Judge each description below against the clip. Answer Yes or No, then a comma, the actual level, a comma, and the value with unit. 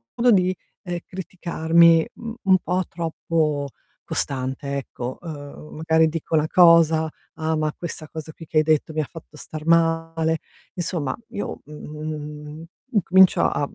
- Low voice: No, medium, 160 Hz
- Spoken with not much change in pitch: Yes, narrow, 1.8 semitones